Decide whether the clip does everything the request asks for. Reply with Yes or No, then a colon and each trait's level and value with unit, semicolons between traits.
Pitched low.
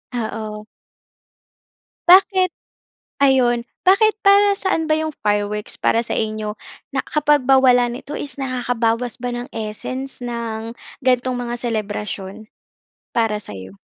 No: high, 240 Hz